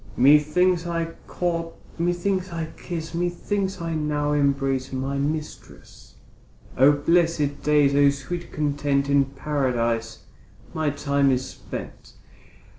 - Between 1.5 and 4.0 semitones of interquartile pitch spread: Yes, average, 3.2 semitones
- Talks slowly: Yes, slow, 115 wpm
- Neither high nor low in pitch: Yes, medium, 150 Hz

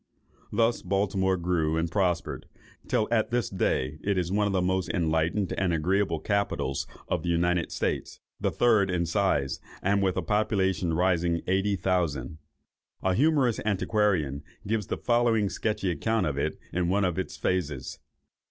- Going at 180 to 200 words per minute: No, average, 160 wpm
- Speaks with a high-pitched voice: No, very low, 95 Hz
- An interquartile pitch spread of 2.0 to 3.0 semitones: No, average, 3.4 semitones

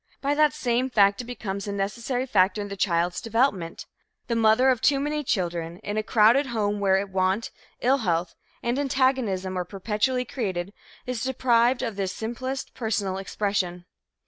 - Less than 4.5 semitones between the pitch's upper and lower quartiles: No, average, 4.8 semitones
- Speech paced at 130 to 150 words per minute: No, average, 165 wpm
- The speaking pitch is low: No, high, 215 Hz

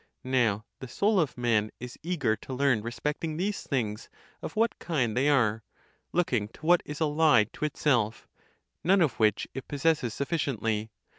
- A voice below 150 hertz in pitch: Yes, low, 135 Hz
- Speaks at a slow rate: No, average, 160 wpm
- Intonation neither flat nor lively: No, wide, 5.7 semitones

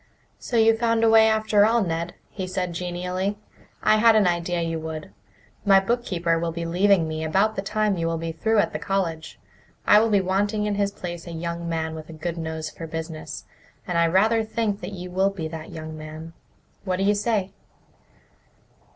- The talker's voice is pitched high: No, medium, 180 Hz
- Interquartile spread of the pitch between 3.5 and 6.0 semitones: Yes, average, 4.0 semitones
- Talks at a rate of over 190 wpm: Yes, fast, 205 wpm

